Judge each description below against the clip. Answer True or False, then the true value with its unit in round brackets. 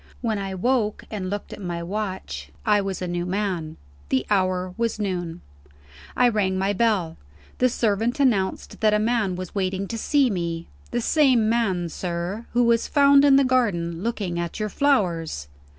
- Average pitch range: True (4.5 semitones)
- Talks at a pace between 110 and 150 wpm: False (175 wpm)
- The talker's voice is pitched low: False (200 Hz)